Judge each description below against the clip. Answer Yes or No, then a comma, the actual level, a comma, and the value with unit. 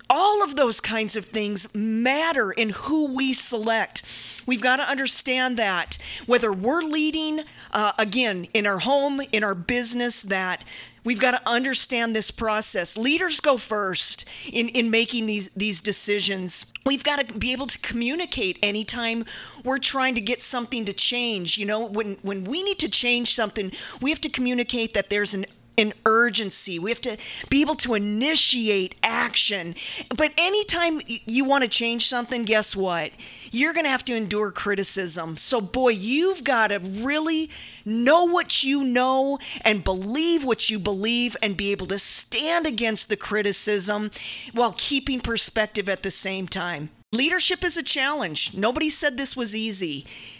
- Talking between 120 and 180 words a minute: Yes, average, 165 wpm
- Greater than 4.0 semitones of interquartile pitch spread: Yes, average, 4.6 semitones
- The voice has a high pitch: Yes, high, 235 Hz